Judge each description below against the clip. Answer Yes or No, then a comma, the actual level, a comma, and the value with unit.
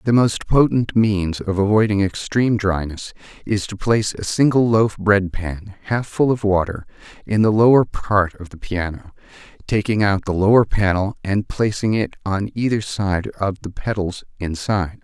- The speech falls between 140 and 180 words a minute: Yes, average, 170 wpm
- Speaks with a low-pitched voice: Yes, low, 100 Hz